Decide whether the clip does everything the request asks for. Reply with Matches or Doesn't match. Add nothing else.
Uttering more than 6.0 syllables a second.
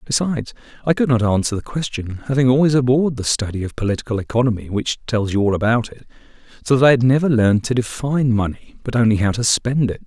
Matches